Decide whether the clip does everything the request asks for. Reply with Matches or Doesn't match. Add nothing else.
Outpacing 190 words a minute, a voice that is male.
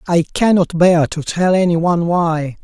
Doesn't match